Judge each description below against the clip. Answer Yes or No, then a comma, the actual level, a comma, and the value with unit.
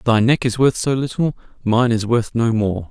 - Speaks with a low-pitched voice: Yes, low, 120 Hz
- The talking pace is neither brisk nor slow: No, fast, 250 wpm